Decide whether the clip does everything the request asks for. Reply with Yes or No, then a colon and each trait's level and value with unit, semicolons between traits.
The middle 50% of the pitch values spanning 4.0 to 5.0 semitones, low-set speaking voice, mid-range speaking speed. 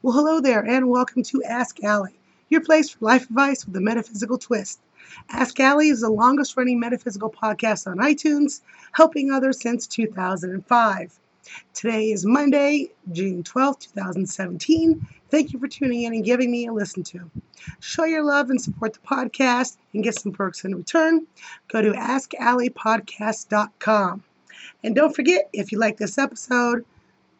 No: average, 4.5 semitones; high, 240 Hz; average, 160 wpm